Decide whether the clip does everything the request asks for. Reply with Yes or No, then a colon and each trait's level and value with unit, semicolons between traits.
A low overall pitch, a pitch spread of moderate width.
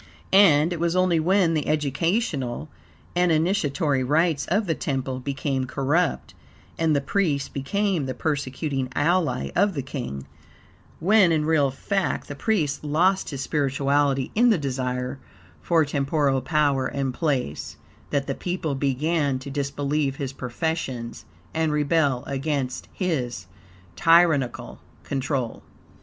No: medium, 145 Hz; average, 3.5 semitones